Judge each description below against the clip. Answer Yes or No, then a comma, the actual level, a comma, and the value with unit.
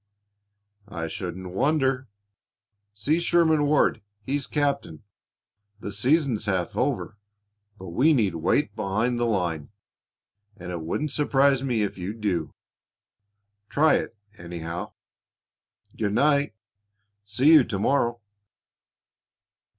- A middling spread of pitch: No, wide, 7.0 semitones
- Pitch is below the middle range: Yes, low, 110 Hz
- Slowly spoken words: Yes, slow, 110 wpm